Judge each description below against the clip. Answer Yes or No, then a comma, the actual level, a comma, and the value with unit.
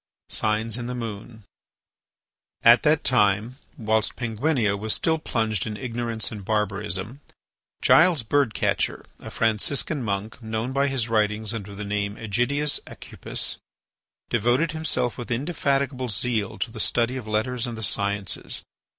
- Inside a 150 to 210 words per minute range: No, average, 140 wpm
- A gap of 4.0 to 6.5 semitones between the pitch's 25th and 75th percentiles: No, average, 3.2 semitones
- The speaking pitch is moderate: No, low, 115 Hz